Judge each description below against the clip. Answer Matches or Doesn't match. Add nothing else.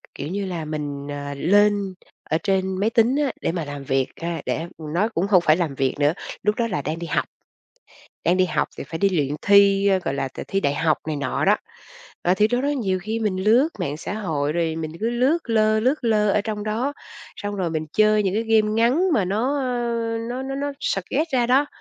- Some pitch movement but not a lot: Doesn't match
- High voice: Matches